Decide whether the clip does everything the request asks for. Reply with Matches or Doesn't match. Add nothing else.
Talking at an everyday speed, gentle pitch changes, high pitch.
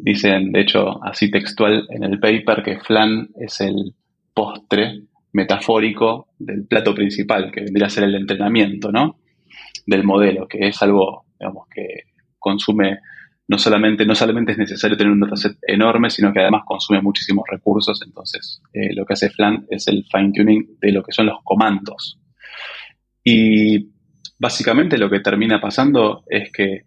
Doesn't match